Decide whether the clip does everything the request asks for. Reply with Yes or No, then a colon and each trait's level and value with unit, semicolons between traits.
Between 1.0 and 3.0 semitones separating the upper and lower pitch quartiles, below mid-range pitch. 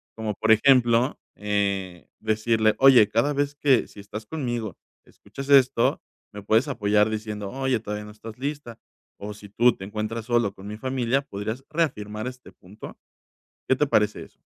No: average, 3.6 semitones; low, 110 Hz